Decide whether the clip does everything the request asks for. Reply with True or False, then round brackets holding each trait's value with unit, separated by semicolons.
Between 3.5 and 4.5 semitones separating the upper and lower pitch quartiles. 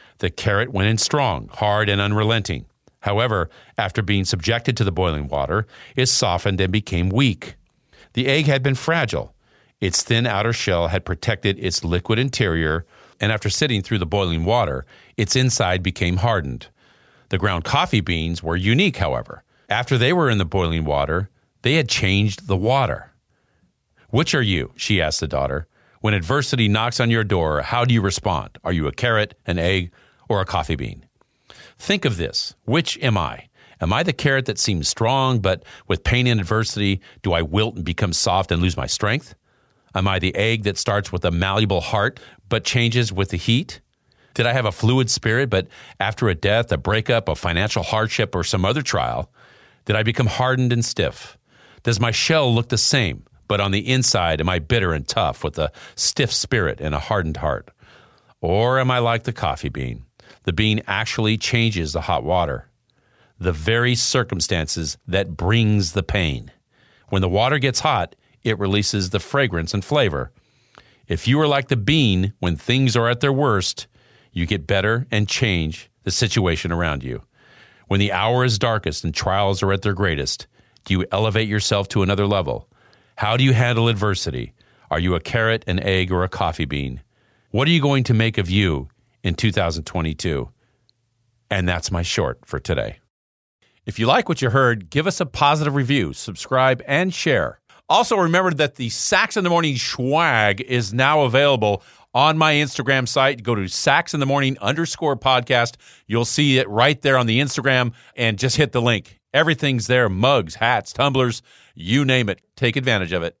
False (5.1 semitones)